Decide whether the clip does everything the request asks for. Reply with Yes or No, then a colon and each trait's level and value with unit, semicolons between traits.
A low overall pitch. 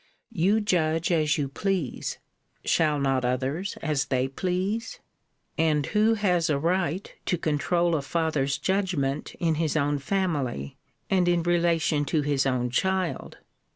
No: medium, 160 Hz